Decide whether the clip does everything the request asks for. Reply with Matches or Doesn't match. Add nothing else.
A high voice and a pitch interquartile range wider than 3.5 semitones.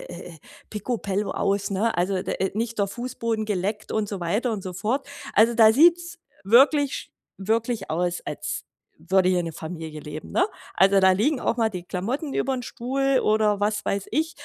Matches